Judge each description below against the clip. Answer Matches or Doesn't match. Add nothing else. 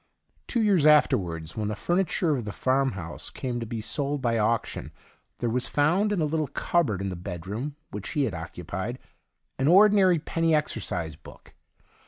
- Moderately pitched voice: Doesn't match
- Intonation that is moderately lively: Doesn't match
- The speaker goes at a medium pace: Matches